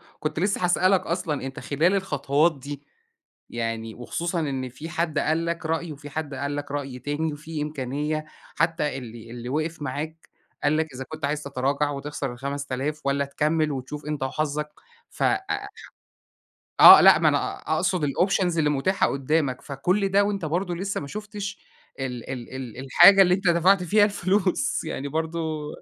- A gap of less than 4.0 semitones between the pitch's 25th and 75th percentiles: Yes, average, 3.6 semitones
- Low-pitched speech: No, medium, 150 Hz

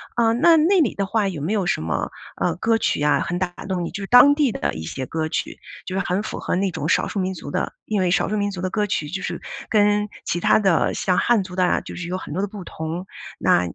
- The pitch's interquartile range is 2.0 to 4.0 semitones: Yes, average, 3.3 semitones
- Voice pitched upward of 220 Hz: No, high, 190 Hz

